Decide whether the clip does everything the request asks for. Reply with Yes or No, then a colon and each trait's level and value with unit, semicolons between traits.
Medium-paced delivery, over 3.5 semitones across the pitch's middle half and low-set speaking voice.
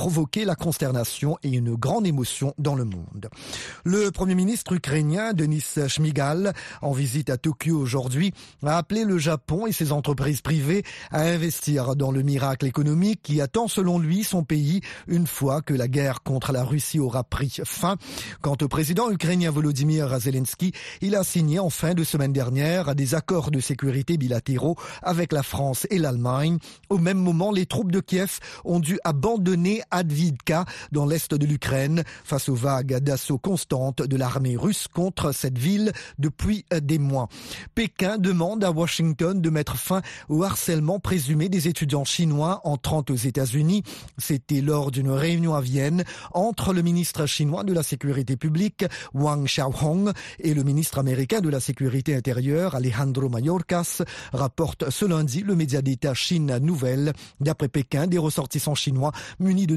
No: average, 165 wpm; average, 4.1 semitones; medium, 155 Hz